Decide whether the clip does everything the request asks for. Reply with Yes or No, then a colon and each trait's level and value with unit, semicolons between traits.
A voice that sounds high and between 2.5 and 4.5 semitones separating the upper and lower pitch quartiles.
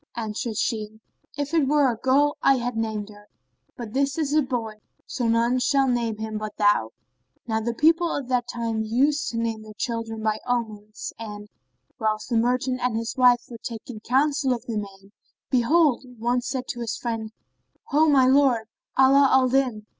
Yes: high, 235 Hz; average, 3.3 semitones